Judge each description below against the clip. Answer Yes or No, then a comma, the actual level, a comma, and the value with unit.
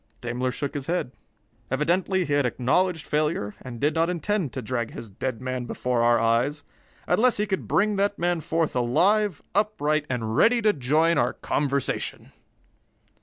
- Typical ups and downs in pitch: No, wide, 6.2 semitones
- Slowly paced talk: No, average, 165 wpm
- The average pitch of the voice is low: No, medium, 150 Hz